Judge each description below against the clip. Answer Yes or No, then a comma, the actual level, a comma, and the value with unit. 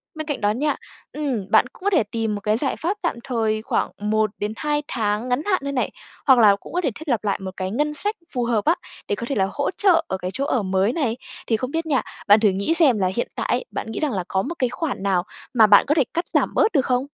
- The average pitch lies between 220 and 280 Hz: Yes, high, 245 Hz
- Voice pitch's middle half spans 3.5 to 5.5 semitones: No, wide, 6.2 semitones